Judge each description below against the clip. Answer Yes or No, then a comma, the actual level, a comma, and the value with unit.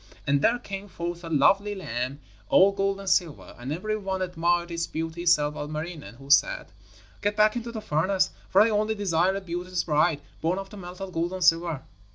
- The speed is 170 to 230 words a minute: Yes, average, 200 wpm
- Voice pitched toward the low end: No, medium, 175 Hz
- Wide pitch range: No, average, 3.4 semitones